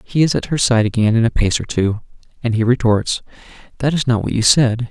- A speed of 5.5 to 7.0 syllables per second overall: Yes, 5.7 syllables/s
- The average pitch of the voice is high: No, low, 115 Hz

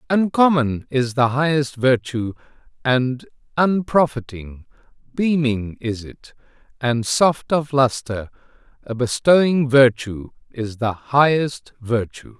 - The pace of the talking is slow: Yes, slow, 100 wpm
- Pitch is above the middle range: No, low, 130 Hz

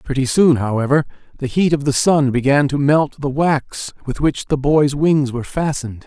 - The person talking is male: Yes, male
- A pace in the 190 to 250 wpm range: Yes, average, 200 wpm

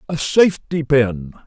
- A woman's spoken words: No, male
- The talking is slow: Yes, slow, 125 wpm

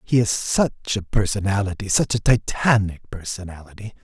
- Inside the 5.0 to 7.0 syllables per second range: Yes, 5.3 syllables/s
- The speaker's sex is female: No, male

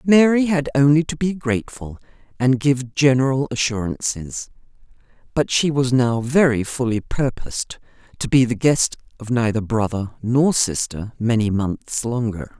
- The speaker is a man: No, female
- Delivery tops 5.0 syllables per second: No, 4.5 syllables/s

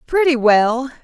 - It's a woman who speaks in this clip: Yes, female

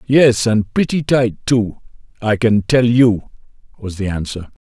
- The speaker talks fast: No, average, 155 wpm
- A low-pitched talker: Yes, low, 115 Hz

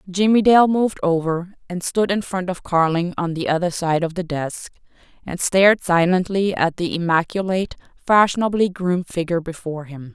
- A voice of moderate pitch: Yes, medium, 180 Hz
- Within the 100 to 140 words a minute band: No, average, 160 wpm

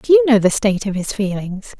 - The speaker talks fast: Yes, fast, 270 wpm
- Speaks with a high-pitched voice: Yes, high, 200 Hz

